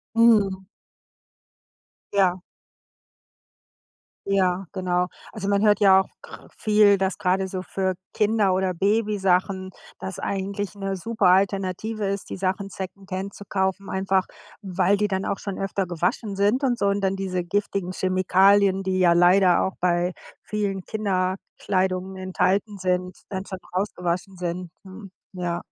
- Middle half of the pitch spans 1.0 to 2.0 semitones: Yes, narrow, 1.5 semitones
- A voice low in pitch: No, high, 190 Hz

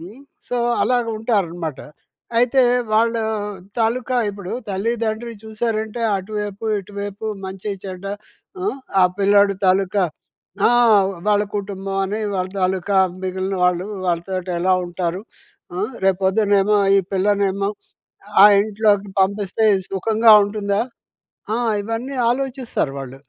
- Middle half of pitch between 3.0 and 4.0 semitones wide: No, narrow, 2.6 semitones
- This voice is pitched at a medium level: No, high, 200 Hz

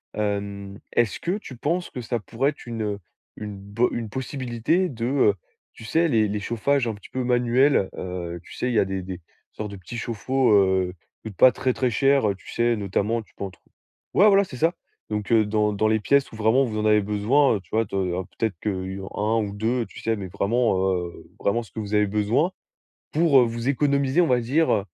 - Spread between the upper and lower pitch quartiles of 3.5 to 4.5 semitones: Yes, average, 4.1 semitones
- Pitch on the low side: Yes, low, 115 Hz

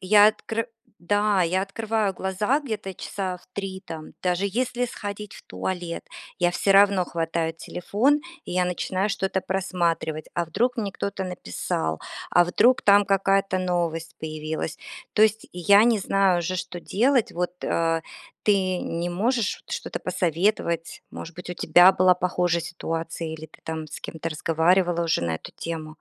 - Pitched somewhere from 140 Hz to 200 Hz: Yes, medium, 185 Hz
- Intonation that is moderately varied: Yes, average, 3.2 semitones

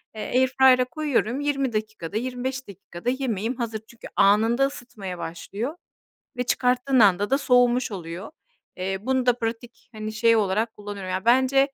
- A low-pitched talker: No, high, 235 Hz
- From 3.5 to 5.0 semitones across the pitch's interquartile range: Yes, average, 3.8 semitones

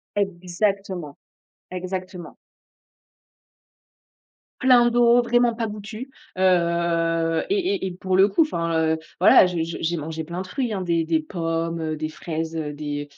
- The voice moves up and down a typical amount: Yes, average, 3.5 semitones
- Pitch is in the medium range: Yes, medium, 175 Hz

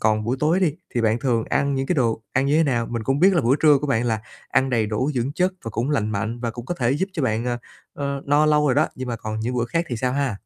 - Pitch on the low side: Yes, low, 130 Hz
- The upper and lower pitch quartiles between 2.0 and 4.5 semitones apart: Yes, average, 3.9 semitones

